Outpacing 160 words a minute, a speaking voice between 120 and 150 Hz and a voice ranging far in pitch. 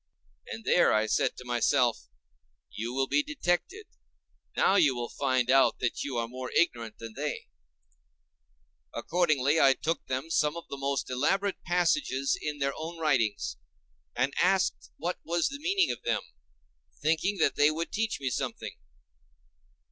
No: average, 155 wpm; medium, 140 Hz; wide, 6.0 semitones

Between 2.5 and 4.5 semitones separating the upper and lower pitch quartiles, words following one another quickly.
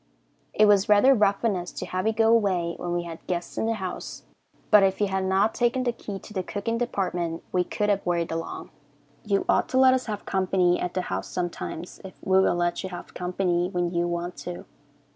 Yes: average, 3.1 semitones; fast, 225 wpm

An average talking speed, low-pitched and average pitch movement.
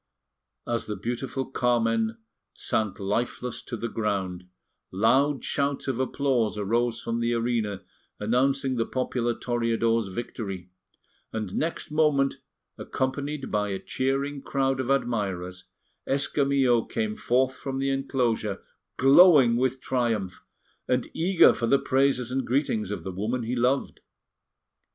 No: slow, 130 wpm; low, 120 Hz; average, 3.4 semitones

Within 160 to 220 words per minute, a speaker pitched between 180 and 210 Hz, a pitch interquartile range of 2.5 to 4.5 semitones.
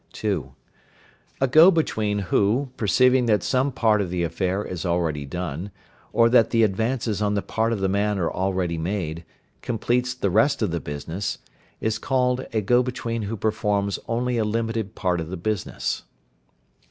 No: average, 170 wpm; low, 105 Hz; average, 4.1 semitones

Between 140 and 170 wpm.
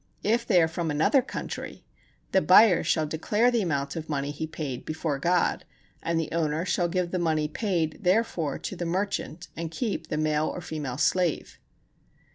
No: average, 180 wpm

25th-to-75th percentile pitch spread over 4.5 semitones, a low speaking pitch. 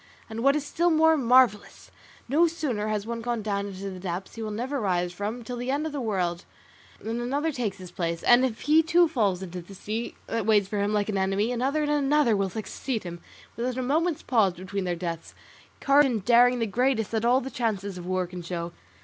No: average, 5.2 semitones; high, 225 Hz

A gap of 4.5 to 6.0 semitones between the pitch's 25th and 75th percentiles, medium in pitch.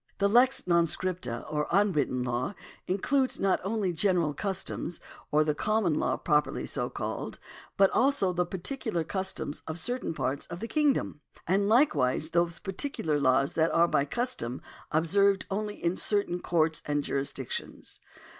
Yes: average, 5.1 semitones; medium, 175 Hz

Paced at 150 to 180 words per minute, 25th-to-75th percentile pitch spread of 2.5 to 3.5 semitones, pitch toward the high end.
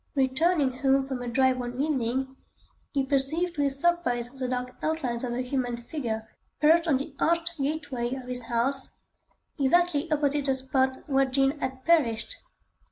Yes: average, 165 wpm; average, 3.0 semitones; very high, 270 Hz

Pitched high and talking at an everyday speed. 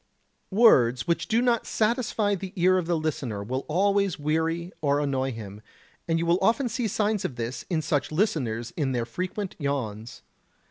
No: medium, 165 Hz; average, 175 wpm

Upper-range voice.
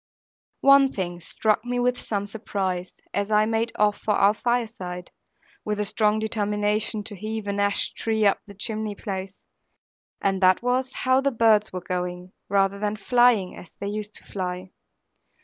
Yes: high, 210 Hz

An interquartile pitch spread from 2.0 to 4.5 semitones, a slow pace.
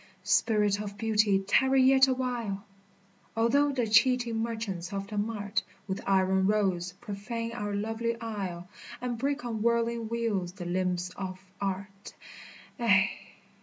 Yes: average, 3.1 semitones; slow, 130 wpm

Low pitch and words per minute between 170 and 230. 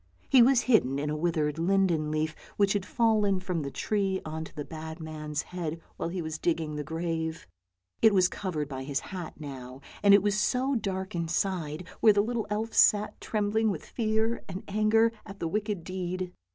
No: medium, 185 Hz; average, 190 wpm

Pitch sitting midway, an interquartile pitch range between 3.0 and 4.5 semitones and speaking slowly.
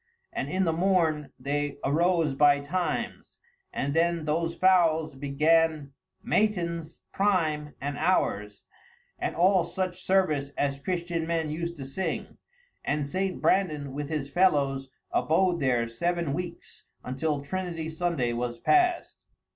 Yes: medium, 160 Hz; average, 3.9 semitones; slow, 130 wpm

